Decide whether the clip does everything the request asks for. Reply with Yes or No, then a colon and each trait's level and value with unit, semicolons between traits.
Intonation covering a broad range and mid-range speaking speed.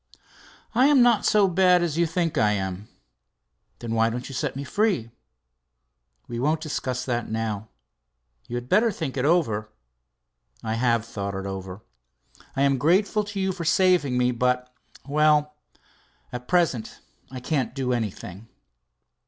Yes: wide, 6.9 semitones; average, 155 wpm